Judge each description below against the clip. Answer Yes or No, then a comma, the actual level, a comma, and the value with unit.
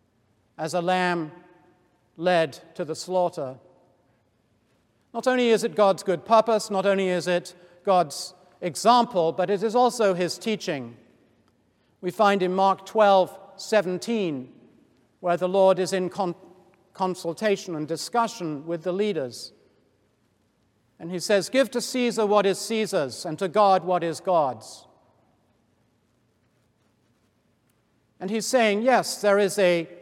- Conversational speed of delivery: No, slow, 130 wpm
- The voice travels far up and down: Yes, wide, 6.3 semitones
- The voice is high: No, medium, 180 Hz